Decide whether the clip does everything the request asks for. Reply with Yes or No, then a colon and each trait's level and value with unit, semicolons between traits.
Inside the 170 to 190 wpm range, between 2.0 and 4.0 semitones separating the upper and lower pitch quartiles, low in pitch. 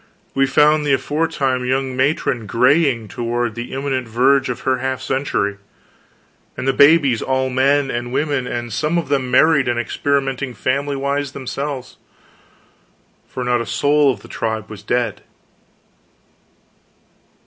No: slow, 135 wpm; narrow, 2.5 semitones; low, 130 Hz